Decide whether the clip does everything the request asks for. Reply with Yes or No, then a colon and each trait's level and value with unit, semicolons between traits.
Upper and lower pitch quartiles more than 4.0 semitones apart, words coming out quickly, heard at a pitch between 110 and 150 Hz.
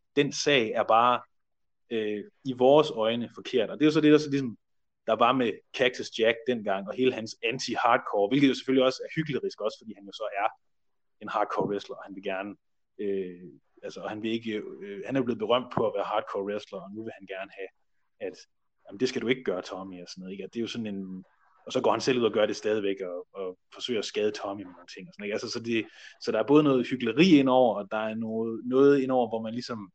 Yes: average, 4.9 semitones; fast, 255 wpm; low, 115 Hz